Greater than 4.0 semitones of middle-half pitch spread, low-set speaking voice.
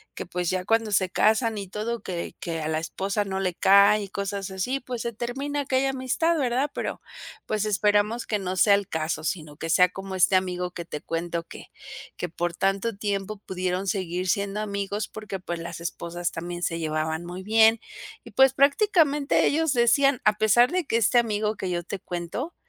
No: average, 4.5 semitones; high, 200 Hz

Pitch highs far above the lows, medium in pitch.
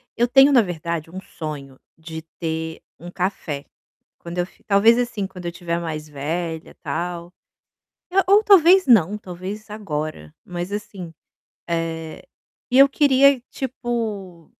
Yes: wide, 5.8 semitones; medium, 180 Hz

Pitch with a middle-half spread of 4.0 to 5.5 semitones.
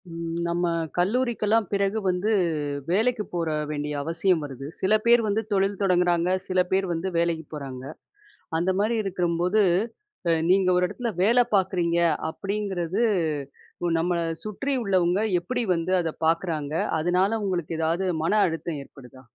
No: average, 3.3 semitones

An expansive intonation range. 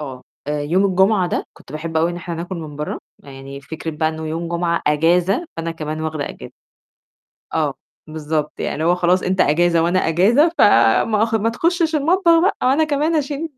Yes: wide, 6.1 semitones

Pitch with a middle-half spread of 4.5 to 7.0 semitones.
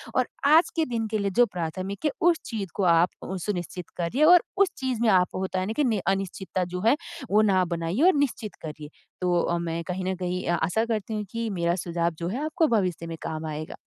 Yes: average, 5.0 semitones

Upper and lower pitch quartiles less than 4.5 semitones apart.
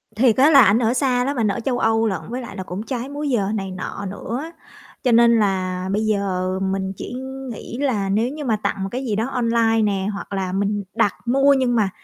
Yes: average, 4.1 semitones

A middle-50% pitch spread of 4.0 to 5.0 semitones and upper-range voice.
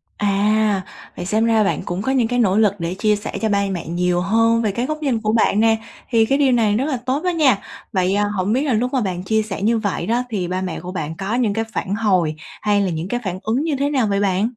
No: average, 3.6 semitones; high, 215 Hz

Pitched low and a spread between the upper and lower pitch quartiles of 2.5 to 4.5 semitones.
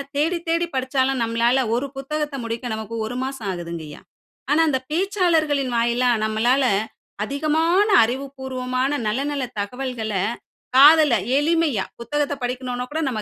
No: very high, 265 Hz; average, 3.9 semitones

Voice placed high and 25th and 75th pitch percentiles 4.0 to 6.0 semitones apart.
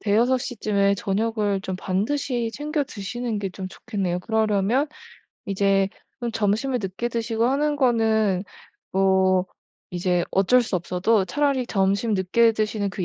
No: high, 210 Hz; average, 3.6 semitones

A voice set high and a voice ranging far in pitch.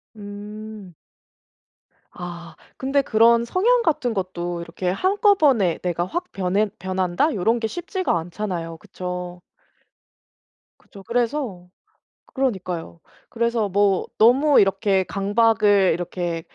No: high, 200 Hz; average, 4.7 semitones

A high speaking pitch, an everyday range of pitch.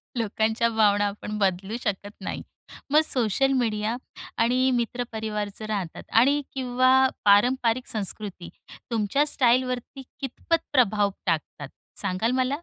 Yes: high, 225 Hz; average, 3.6 semitones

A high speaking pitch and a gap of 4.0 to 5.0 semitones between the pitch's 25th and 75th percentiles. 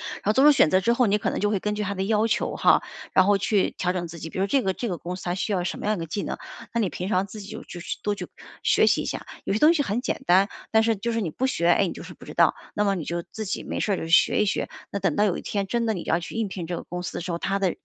No: high, 195 Hz; average, 3.1 semitones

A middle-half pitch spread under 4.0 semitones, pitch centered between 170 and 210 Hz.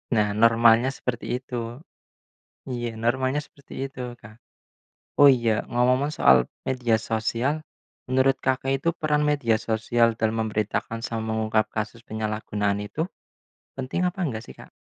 No: average, 3.1 semitones; low, 115 Hz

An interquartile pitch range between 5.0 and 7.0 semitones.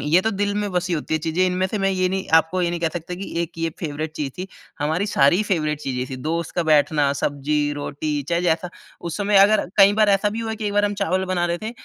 No: average, 4.3 semitones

